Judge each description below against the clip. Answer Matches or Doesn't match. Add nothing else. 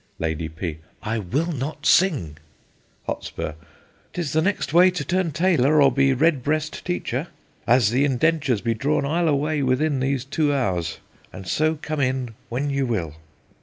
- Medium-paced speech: Matches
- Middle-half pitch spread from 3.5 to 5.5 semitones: Matches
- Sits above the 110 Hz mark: Matches